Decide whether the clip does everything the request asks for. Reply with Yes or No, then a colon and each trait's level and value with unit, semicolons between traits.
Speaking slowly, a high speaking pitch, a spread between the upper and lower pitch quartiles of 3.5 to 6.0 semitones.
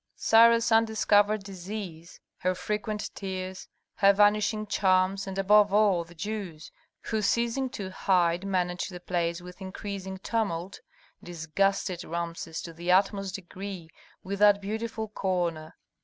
No: slow, 125 wpm; high, 195 Hz; average, 2.8 semitones